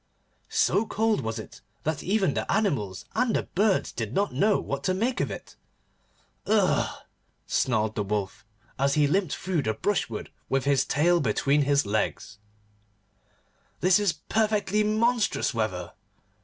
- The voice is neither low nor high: Yes, medium, 155 Hz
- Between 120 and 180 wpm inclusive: Yes, average, 145 wpm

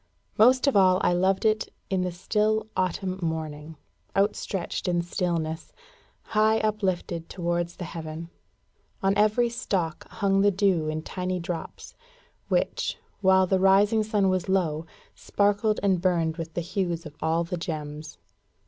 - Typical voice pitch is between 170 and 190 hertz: Yes, medium, 185 Hz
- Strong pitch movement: No, average, 3.2 semitones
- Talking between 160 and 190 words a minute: No, average, 145 wpm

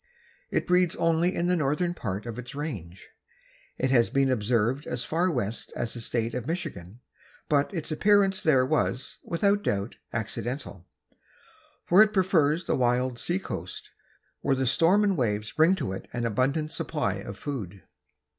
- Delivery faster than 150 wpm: Yes, average, 165 wpm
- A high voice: No, low, 135 Hz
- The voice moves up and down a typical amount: No, wide, 6.3 semitones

